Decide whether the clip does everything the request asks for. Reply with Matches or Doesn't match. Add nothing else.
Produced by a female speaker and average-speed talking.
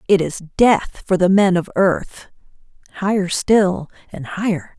Matches